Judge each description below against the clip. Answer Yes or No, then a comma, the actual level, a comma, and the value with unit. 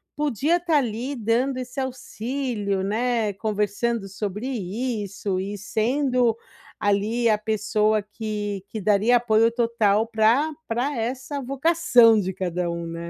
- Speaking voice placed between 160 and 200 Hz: No, high, 225 Hz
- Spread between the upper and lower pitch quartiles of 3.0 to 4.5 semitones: Yes, average, 3.4 semitones